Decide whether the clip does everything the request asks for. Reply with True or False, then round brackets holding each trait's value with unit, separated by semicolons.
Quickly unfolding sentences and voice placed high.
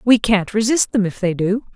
True (240 wpm; 210 Hz)